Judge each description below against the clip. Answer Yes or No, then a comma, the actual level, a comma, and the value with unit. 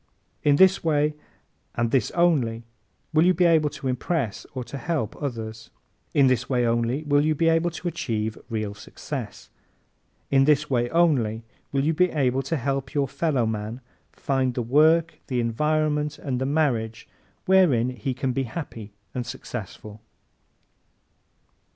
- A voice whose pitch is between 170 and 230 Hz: No, low, 135 Hz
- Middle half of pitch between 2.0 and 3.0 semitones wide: No, average, 4.7 semitones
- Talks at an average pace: Yes, average, 150 wpm